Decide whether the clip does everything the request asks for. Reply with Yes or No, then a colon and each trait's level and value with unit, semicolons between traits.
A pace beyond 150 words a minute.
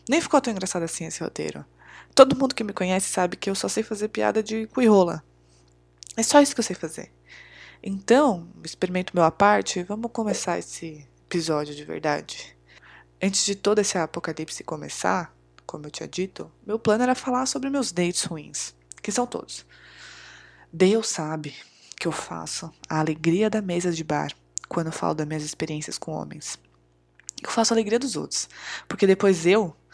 Yes: average, 175 wpm